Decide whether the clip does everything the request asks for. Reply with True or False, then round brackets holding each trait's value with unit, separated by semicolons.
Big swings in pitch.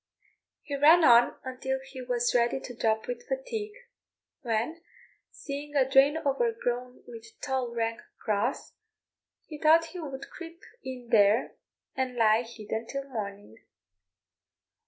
False (4.4 semitones)